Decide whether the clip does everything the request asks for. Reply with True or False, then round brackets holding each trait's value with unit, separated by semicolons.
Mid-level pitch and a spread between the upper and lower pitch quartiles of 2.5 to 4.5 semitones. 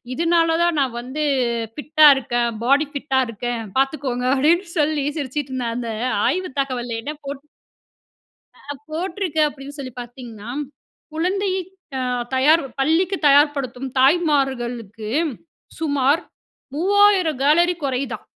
False (280 Hz; 4.1 semitones)